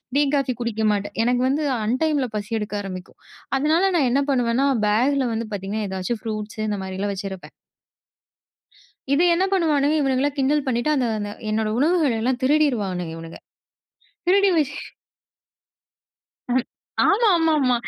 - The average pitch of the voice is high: Yes, high, 245 Hz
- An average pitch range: No, wide, 5.7 semitones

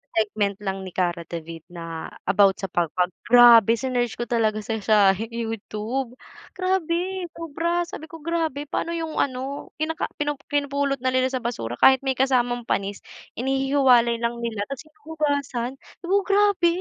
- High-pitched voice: Yes, very high, 255 Hz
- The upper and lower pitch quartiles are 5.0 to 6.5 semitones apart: Yes, wide, 5.6 semitones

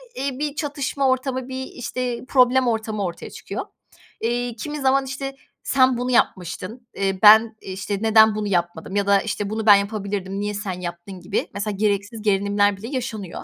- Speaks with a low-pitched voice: No, high, 220 Hz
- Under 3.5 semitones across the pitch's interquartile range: No, average, 4.1 semitones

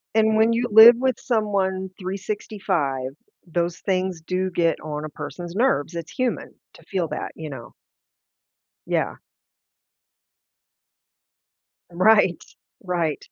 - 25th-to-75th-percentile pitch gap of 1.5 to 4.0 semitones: No, average, 4.4 semitones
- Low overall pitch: No, medium, 185 Hz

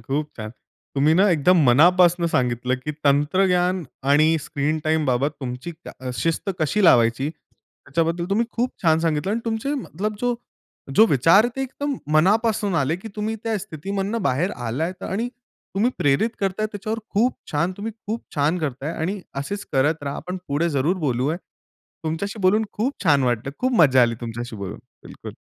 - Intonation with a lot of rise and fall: Yes, wide, 6.3 semitones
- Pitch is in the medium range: Yes, medium, 165 Hz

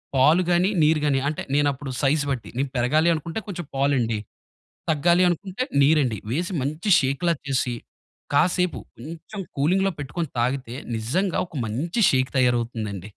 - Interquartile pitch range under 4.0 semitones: No, average, 5.0 semitones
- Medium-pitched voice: Yes, medium, 145 Hz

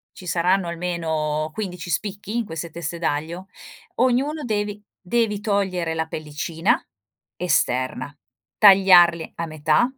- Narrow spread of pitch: No, average, 4.0 semitones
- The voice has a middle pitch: Yes, medium, 175 Hz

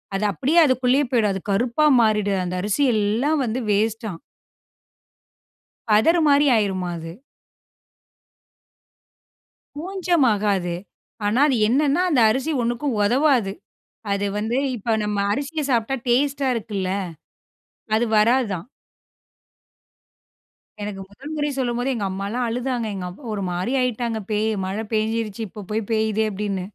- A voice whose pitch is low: No, high, 225 Hz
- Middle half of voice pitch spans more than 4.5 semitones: No, average, 4.2 semitones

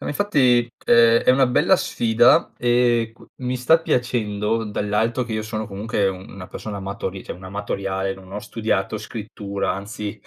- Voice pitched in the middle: No, low, 110 Hz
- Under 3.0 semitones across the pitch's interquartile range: No, average, 3.3 semitones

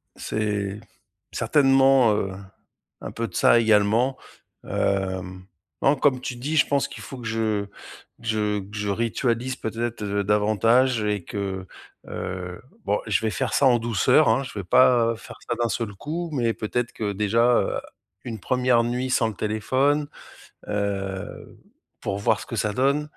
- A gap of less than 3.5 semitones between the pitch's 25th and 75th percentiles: No, average, 3.8 semitones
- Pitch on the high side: No, low, 115 Hz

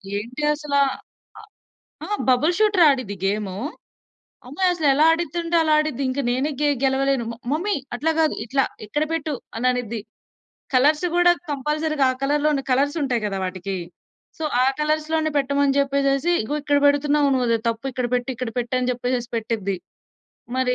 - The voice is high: Yes, very high, 275 Hz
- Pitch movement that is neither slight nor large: Yes, average, 3.5 semitones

